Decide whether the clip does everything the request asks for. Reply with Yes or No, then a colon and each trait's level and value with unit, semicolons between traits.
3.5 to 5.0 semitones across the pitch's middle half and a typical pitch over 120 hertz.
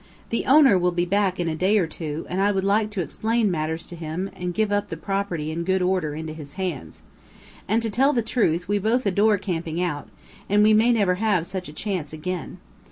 Yes: average, 3.9 semitones; medium, 185 Hz